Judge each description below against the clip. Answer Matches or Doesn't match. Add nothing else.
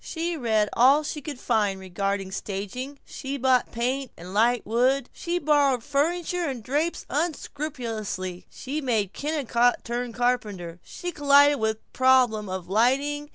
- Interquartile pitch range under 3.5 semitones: Doesn't match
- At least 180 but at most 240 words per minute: Doesn't match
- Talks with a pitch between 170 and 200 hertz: Doesn't match